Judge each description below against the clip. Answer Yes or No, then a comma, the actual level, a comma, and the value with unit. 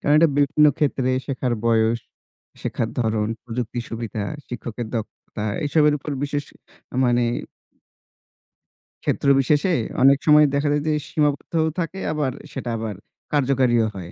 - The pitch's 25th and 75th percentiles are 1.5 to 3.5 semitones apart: No, average, 4.1 semitones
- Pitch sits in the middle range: No, low, 130 Hz